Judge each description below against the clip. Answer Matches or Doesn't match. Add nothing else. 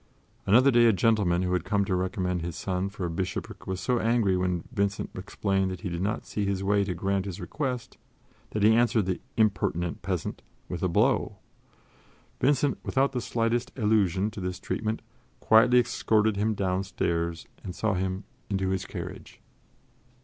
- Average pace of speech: Matches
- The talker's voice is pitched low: Matches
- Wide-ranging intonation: Doesn't match